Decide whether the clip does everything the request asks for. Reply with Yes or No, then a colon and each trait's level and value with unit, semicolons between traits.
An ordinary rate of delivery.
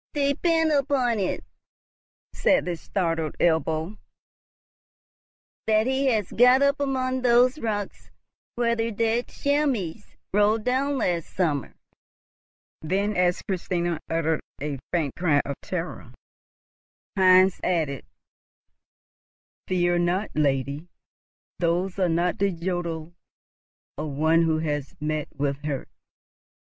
No: slow, 110 wpm